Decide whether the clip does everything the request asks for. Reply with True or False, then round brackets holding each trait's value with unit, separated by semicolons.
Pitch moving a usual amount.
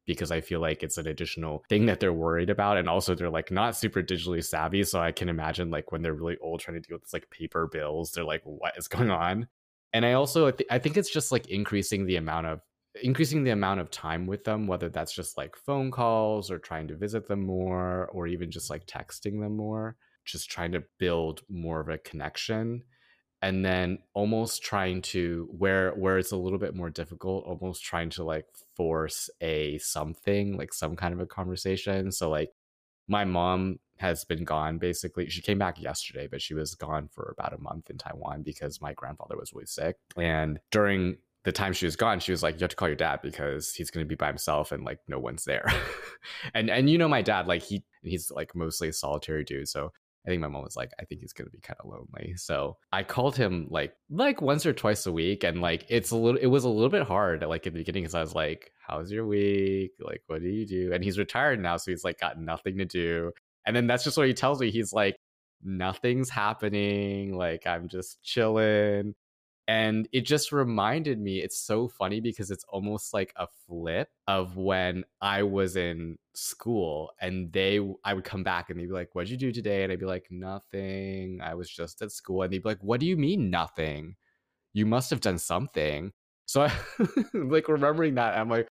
True (4.1 semitones)